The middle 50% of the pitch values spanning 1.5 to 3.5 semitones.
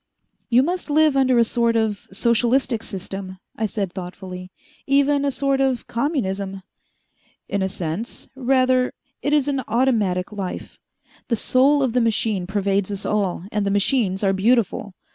No: average, 5.2 semitones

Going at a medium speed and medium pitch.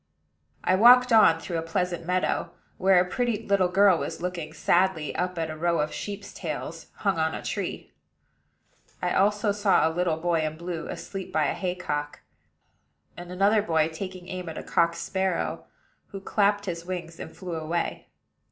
Yes: average, 175 wpm; medium, 180 Hz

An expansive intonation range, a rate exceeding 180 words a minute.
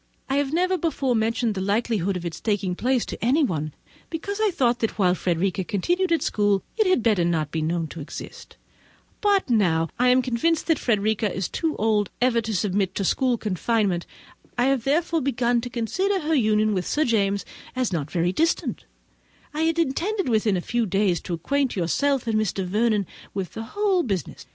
Yes: wide, 6.4 semitones; average, 195 wpm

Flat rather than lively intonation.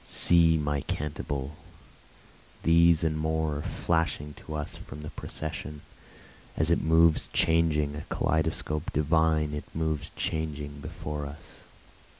Yes: narrow, 1.5 semitones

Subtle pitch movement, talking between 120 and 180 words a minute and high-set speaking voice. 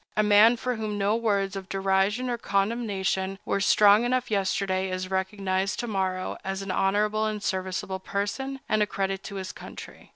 Yes: narrow, 2.0 semitones; average, 175 wpm; high, 200 Hz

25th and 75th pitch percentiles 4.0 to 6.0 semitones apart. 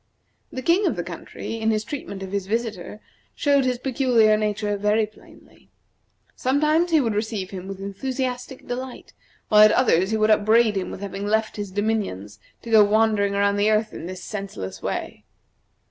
No: average, 3.1 semitones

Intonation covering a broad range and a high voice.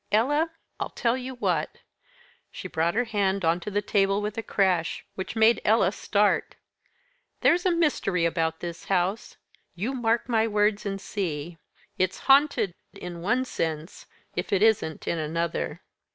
No: average, 4.7 semitones; high, 200 Hz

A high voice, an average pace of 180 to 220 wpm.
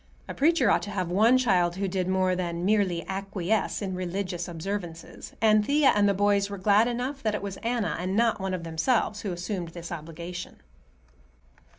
Yes: high, 195 Hz; average, 190 wpm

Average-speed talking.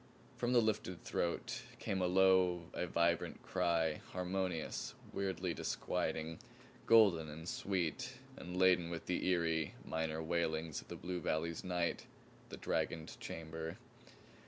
No: slow, 130 wpm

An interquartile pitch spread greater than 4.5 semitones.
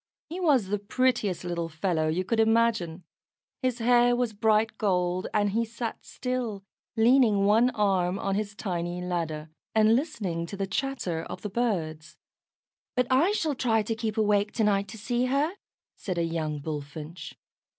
Yes: average, 5.2 semitones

